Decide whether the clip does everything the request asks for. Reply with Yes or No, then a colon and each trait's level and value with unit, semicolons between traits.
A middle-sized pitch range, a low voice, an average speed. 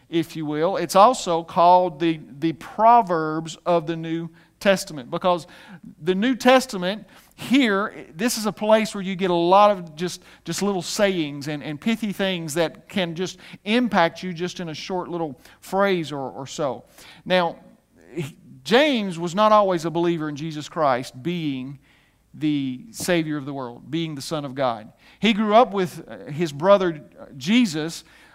No: average, 3.8 semitones; medium, 175 Hz; average, 165 wpm